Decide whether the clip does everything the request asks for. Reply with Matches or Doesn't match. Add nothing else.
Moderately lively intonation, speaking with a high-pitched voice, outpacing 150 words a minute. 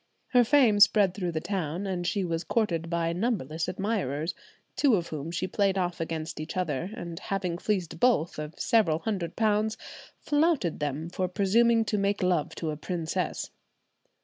Doesn't match